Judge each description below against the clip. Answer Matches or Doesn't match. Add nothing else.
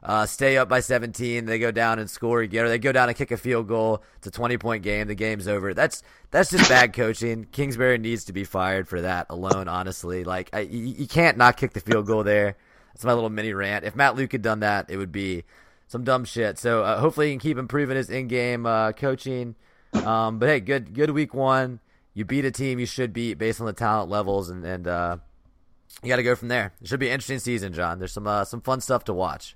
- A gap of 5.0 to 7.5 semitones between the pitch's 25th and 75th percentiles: Doesn't match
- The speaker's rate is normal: Doesn't match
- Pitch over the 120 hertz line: Doesn't match